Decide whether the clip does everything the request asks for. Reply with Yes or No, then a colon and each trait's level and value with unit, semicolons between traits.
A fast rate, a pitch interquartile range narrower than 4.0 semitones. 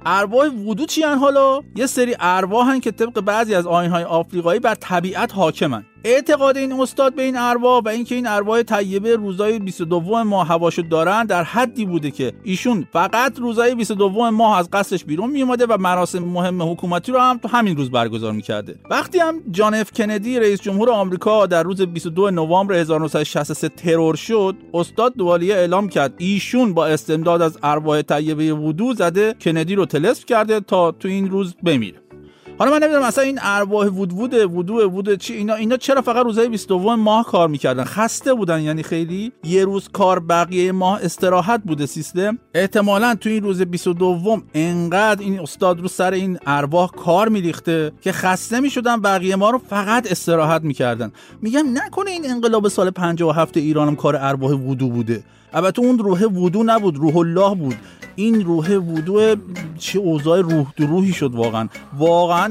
No: fast, 175 wpm; average, 5.0 semitones